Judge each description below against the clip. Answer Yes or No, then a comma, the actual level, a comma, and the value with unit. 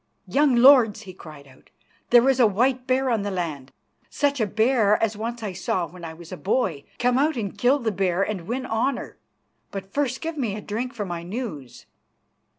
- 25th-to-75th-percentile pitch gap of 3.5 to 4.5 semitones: No, wide, 5.5 semitones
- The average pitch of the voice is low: No, high, 220 Hz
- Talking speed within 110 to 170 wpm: No, fast, 205 wpm